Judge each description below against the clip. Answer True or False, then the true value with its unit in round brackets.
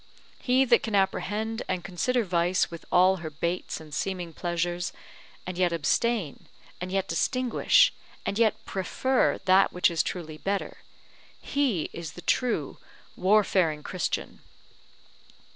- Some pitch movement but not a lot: True (3.9 semitones)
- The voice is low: False (185 Hz)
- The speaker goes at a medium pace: False (130 wpm)